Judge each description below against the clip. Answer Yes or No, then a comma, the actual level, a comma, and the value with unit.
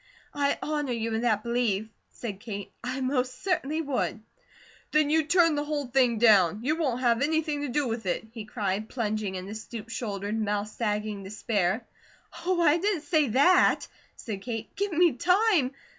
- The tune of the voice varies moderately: No, wide, 5.7 semitones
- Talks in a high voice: Yes, high, 245 Hz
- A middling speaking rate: Yes, average, 175 wpm